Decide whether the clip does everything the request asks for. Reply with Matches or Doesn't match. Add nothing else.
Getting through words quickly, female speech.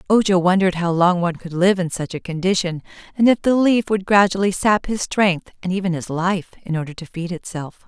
Matches